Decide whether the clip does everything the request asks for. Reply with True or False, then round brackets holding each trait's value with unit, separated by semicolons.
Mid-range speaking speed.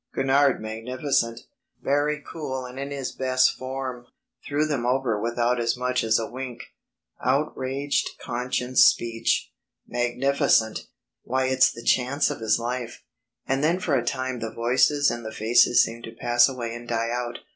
True (155 wpm)